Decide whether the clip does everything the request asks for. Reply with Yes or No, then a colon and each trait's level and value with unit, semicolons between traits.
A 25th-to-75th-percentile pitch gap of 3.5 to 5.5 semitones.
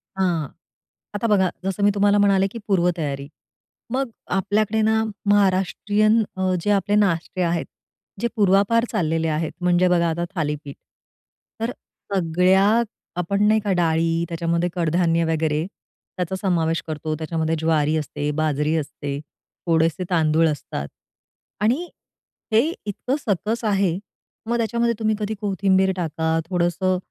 Yes: average, 4.0 semitones